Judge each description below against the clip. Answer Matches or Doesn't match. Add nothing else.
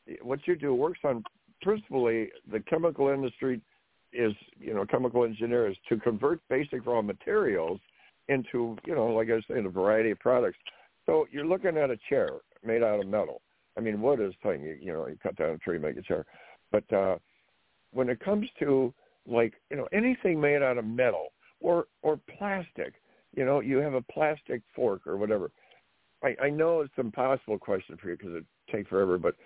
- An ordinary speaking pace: Matches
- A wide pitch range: Matches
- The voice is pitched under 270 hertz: Matches